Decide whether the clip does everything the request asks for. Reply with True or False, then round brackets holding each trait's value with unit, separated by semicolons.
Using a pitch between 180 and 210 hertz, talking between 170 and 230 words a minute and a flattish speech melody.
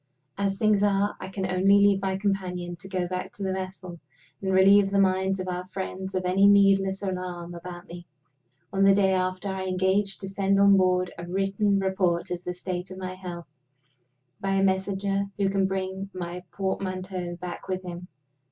True (190 Hz; 190 wpm; 1.3 semitones)